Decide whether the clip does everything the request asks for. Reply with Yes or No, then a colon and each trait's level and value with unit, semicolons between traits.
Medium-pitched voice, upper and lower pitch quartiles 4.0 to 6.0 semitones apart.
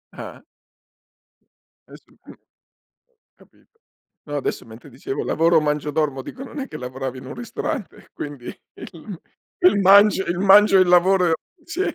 Yes: medium, 175 Hz; wide, 5.6 semitones